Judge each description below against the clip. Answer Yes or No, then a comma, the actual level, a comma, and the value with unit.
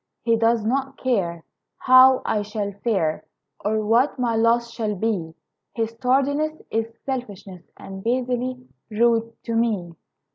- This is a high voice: Yes, high, 230 Hz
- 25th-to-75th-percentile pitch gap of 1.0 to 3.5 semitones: Yes, average, 3.2 semitones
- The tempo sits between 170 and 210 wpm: No, slow, 135 wpm